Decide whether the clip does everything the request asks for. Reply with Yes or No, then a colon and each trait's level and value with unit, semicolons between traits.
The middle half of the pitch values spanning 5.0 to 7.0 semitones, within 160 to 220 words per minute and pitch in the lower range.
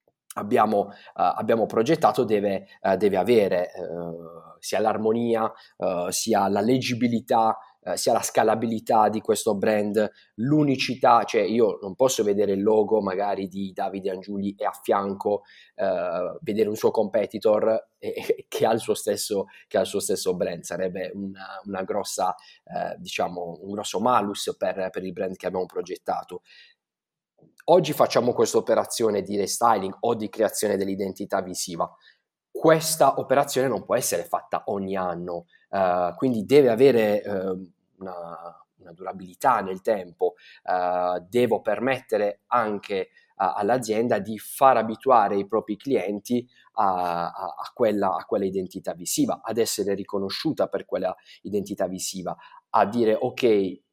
No: average, 5.3 semitones; average, 140 wpm; low, 110 Hz